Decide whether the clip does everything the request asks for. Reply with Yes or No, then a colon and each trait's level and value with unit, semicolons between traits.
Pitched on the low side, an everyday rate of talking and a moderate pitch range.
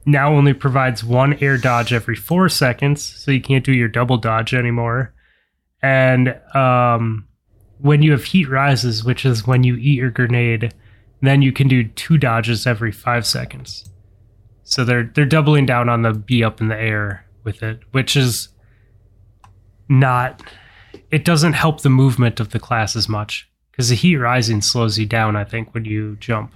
Yes: low, 120 Hz; average, 180 wpm; average, 3.4 semitones